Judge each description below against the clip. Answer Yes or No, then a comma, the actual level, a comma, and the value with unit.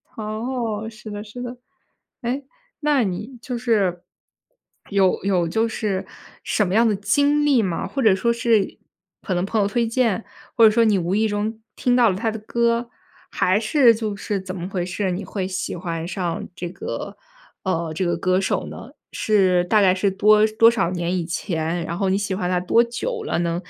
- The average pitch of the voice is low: No, high, 205 Hz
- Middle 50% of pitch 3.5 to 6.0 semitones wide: Yes, average, 3.8 semitones